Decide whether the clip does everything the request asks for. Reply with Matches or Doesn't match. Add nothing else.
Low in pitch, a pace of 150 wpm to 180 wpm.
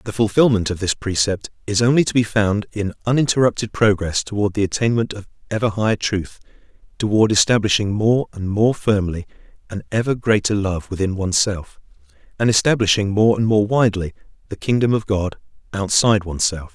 Matches